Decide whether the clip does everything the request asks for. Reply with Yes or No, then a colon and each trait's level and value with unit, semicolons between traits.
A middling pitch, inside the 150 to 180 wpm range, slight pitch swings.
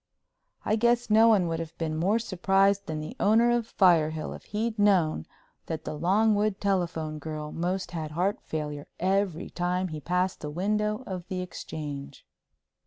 No: medium, 180 Hz; average, 165 wpm; average, 4.6 semitones